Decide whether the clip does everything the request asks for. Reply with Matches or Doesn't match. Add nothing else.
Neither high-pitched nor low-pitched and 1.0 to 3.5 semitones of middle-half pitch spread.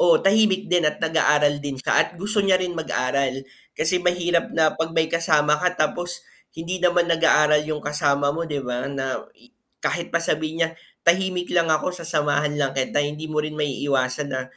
Matches